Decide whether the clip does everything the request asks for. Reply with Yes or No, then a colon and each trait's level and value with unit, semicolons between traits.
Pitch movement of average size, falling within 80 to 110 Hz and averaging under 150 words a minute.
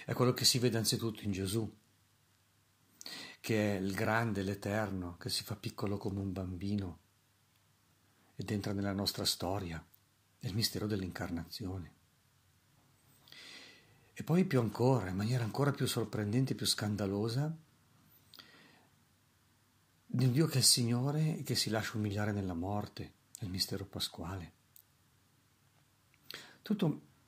Yes: average, 3.9 semitones; low, 105 Hz; average, 125 wpm